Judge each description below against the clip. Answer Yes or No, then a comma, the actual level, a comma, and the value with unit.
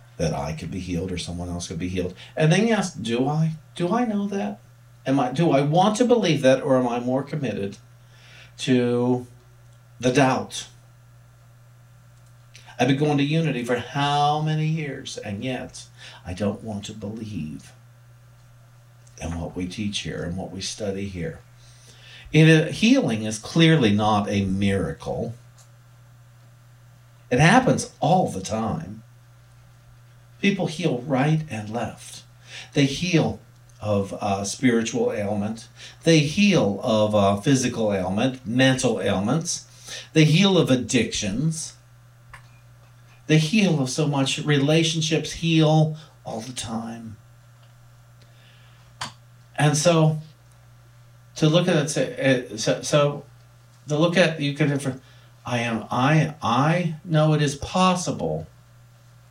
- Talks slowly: Yes, slow, 130 wpm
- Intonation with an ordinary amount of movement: Yes, average, 3.7 semitones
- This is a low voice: Yes, low, 120 Hz